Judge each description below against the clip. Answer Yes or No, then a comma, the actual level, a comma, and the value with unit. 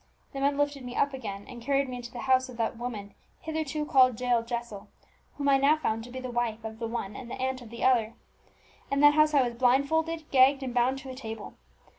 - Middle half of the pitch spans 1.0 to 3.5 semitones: Yes, average, 2.9 semitones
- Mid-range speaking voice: No, very high, 255 Hz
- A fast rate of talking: Yes, fast, 240 wpm